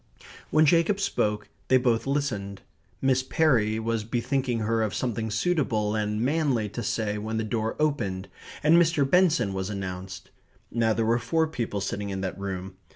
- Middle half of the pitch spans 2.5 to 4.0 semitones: No, average, 4.9 semitones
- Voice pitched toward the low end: Yes, low, 115 Hz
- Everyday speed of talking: Yes, average, 165 wpm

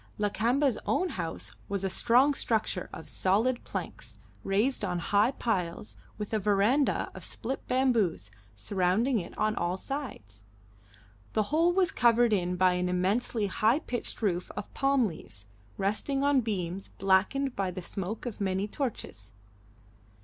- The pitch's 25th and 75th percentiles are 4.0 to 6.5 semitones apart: Yes, average, 5.2 semitones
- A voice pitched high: Yes, high, 210 Hz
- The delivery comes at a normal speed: Yes, average, 145 wpm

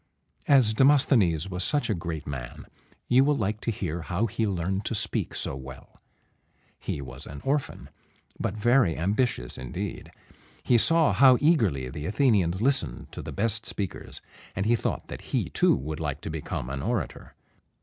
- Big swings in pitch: Yes, wide, 7.5 semitones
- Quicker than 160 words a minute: Yes, average, 170 wpm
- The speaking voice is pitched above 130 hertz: No, low, 100 Hz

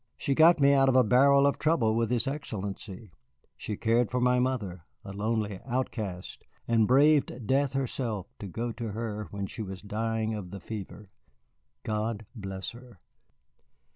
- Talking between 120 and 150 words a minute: No, average, 165 wpm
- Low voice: Yes, low, 115 Hz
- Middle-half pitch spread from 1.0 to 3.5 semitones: No, average, 4.0 semitones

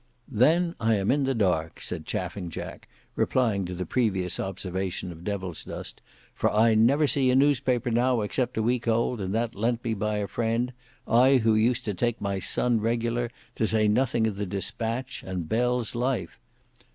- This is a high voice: No, low, 115 Hz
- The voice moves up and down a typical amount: Yes, average, 3.6 semitones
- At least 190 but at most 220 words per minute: No, average, 175 wpm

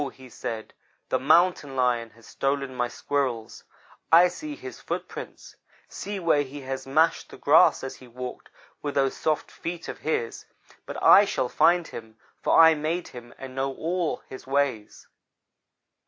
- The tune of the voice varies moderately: Yes, average, 4.5 semitones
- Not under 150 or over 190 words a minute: Yes, average, 160 wpm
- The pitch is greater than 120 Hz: Yes, low, 135 Hz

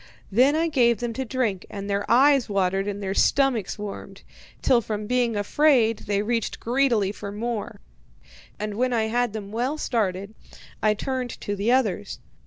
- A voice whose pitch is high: Yes, high, 225 Hz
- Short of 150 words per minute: No, average, 170 wpm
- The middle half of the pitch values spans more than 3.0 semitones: Yes, average, 3.6 semitones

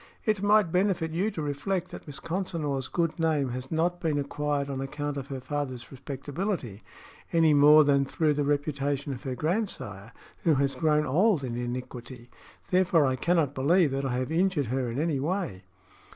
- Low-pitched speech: No, medium, 145 Hz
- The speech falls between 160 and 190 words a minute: Yes, average, 180 wpm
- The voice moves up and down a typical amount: Yes, average, 3.9 semitones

